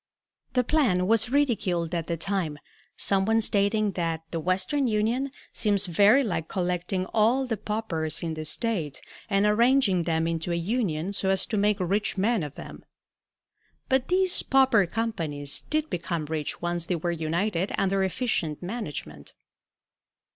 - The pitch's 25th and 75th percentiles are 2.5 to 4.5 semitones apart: No, average, 5.0 semitones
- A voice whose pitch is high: Yes, high, 195 Hz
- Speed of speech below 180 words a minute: Yes, average, 155 wpm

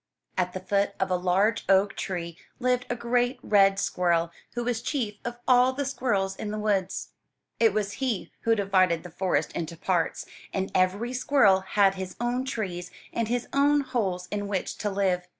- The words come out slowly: No, average, 185 wpm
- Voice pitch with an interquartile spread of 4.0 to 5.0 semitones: Yes, average, 4.4 semitones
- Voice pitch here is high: Yes, high, 200 Hz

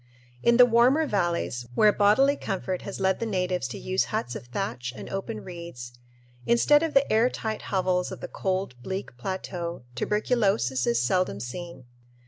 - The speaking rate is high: No, average, 165 wpm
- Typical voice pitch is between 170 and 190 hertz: Yes, medium, 185 Hz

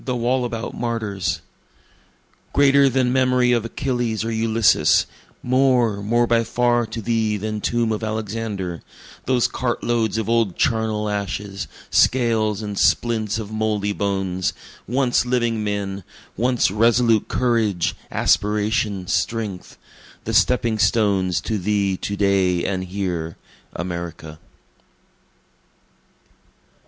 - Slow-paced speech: Yes, slow, 115 wpm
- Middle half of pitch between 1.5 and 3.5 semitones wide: Yes, average, 2.9 semitones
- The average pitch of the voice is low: Yes, low, 110 Hz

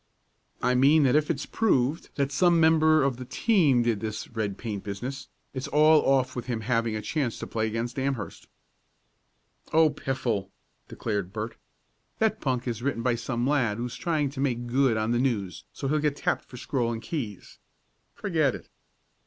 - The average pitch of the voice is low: Yes, low, 130 Hz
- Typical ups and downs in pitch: Yes, average, 4.1 semitones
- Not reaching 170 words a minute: No, average, 180 wpm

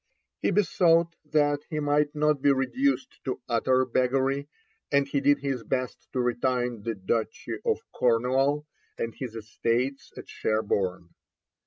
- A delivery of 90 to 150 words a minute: Yes, average, 140 wpm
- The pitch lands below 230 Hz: Yes, low, 135 Hz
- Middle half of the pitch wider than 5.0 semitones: No, average, 3.3 semitones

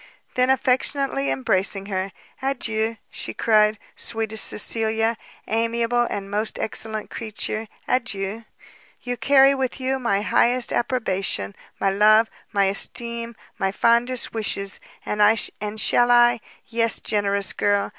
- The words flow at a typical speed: No, slow, 115 wpm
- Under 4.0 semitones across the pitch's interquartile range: Yes, average, 2.9 semitones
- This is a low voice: No, high, 220 Hz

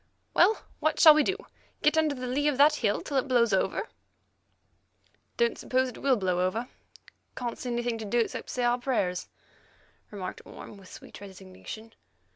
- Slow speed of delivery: No, average, 175 wpm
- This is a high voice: Yes, high, 240 Hz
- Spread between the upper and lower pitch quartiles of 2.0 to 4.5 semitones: No, wide, 5.4 semitones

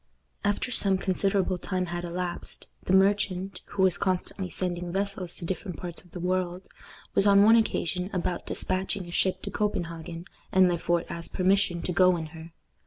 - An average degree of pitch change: No, narrow, 1.9 semitones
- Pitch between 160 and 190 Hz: Yes, medium, 185 Hz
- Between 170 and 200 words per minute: Yes, average, 175 wpm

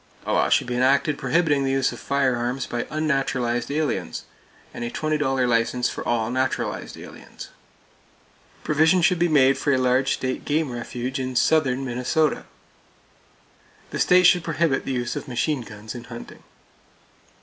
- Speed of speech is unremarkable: Yes, average, 155 wpm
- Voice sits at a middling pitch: No, low, 130 Hz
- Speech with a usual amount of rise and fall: Yes, average, 3.7 semitones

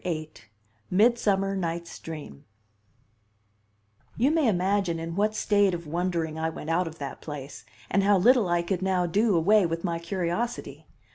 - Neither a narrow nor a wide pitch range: Yes, average, 3.6 semitones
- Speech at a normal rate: Yes, average, 155 wpm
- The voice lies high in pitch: No, medium, 175 Hz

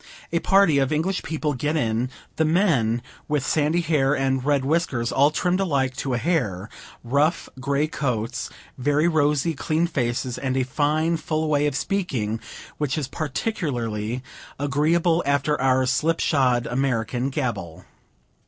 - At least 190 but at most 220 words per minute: No, average, 145 wpm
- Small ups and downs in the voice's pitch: No, average, 3.7 semitones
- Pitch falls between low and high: Yes, medium, 145 Hz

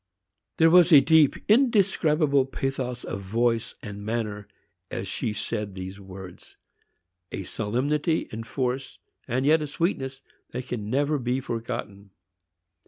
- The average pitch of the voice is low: Yes, low, 125 Hz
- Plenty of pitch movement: Yes, wide, 5.9 semitones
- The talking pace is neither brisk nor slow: No, slow, 125 wpm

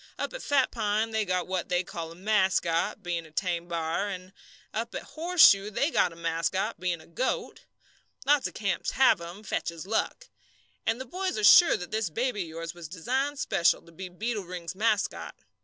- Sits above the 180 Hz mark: Yes, high, 190 Hz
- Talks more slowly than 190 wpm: No, average, 195 wpm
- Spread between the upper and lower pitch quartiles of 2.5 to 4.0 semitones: No, average, 4.9 semitones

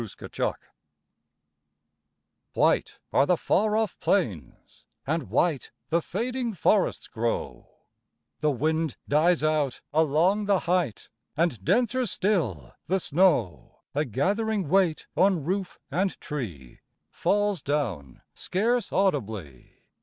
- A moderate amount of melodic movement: No, wide, 6.5 semitones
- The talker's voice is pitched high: No, medium, 165 Hz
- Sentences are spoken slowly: Yes, slow, 110 wpm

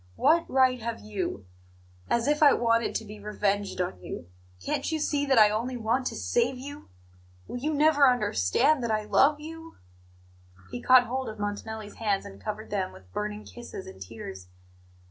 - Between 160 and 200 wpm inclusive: Yes, average, 180 wpm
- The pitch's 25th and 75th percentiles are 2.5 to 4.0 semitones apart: No, average, 4.6 semitones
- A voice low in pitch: No, high, 230 Hz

